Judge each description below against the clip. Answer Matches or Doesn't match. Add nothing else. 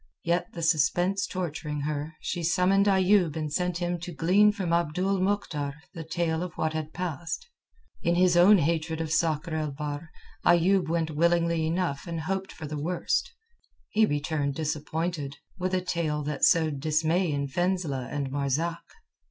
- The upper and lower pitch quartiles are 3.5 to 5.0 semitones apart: Doesn't match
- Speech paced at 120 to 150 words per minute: Doesn't match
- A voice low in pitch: Doesn't match